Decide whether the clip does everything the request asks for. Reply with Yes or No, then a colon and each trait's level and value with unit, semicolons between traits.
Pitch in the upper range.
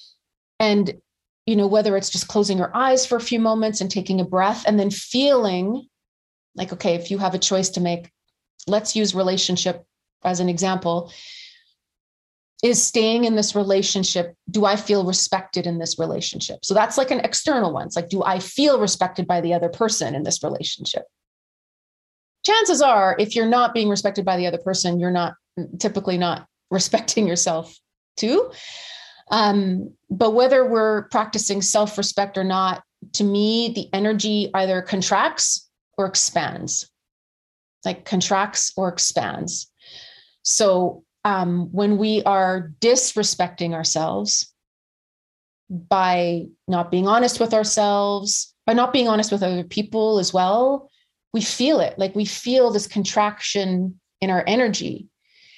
Yes: high, 200 Hz